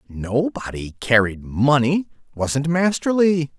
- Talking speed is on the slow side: Yes, slow, 85 wpm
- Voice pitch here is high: No, medium, 140 Hz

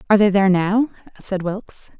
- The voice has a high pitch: Yes, high, 200 Hz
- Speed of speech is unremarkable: Yes, average, 180 wpm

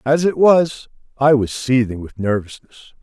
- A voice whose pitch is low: Yes, low, 130 Hz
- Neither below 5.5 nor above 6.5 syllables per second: No, 4.7 syllables/s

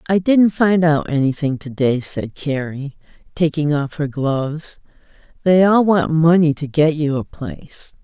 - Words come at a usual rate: Yes, average, 165 wpm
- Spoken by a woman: Yes, female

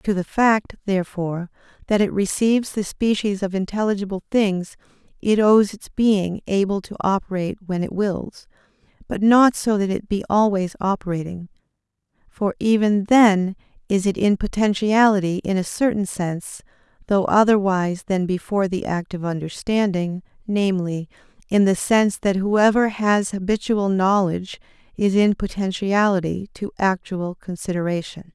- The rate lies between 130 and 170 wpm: Yes, slow, 135 wpm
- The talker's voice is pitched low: No, high, 195 Hz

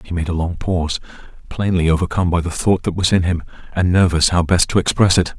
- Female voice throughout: No, male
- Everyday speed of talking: No, fast, 235 wpm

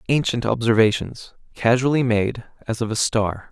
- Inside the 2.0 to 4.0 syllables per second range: Yes, 2.9 syllables/s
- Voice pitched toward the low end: Yes, low, 115 Hz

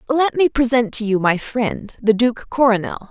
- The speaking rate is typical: Yes, average, 195 wpm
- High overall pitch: Yes, high, 235 Hz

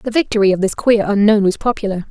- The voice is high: Yes, high, 205 Hz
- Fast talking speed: Yes, fast, 230 wpm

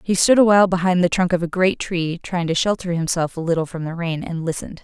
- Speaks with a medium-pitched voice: Yes, medium, 175 Hz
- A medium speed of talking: No, fast, 275 wpm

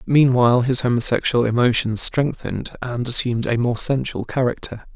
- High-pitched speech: No, low, 120 Hz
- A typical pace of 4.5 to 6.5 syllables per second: Yes, 5.3 syllables/s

